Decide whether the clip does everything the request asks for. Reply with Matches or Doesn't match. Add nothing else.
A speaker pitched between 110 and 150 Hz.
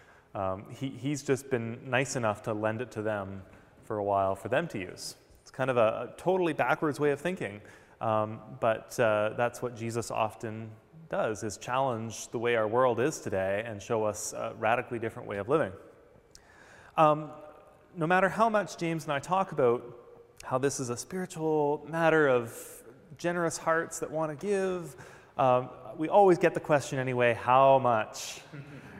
Matches